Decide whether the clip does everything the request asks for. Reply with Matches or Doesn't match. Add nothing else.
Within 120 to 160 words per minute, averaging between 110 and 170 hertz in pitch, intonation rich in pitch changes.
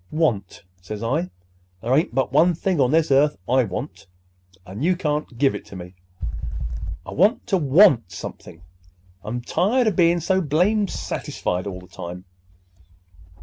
Matches